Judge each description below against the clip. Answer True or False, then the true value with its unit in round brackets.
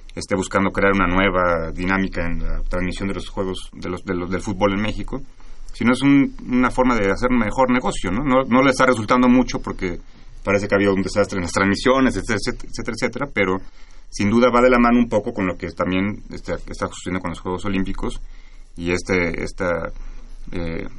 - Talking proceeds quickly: True (210 wpm)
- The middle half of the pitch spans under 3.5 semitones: False (5.2 semitones)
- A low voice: True (100 Hz)